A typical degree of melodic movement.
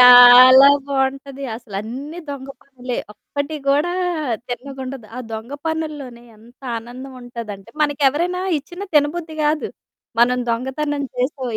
Yes: average, 3.1 semitones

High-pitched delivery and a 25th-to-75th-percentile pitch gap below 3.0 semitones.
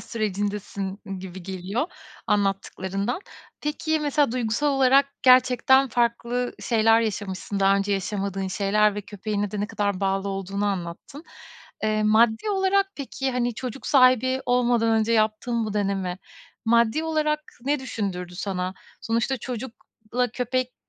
No: high, 220 Hz; average, 4.2 semitones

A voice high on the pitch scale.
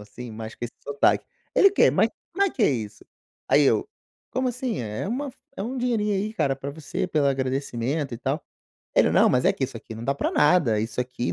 No: medium, 140 Hz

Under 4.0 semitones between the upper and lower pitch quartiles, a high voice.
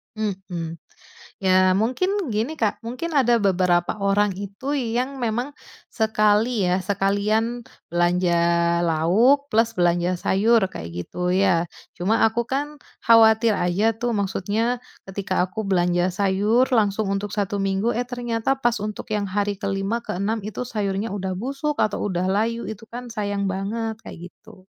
Yes: average, 3.4 semitones; high, 210 Hz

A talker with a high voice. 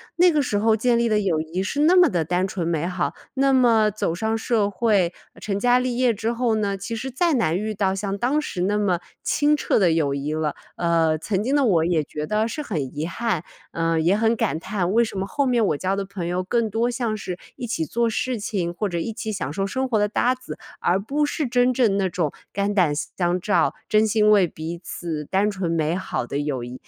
Yes: high, 200 Hz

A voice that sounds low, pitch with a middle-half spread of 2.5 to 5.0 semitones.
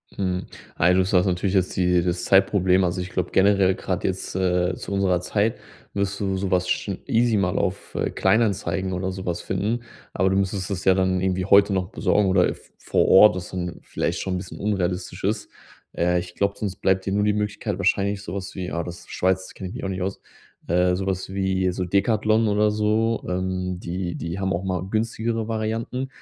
No: very low, 95 Hz; narrow, 1.8 semitones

